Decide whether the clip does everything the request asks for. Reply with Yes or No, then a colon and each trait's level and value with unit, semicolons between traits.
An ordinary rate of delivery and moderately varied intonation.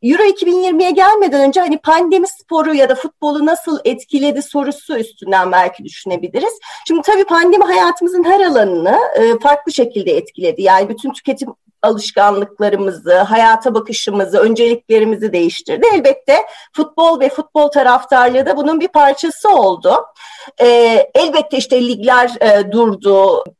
No: average, 120 wpm; wide, 6.9 semitones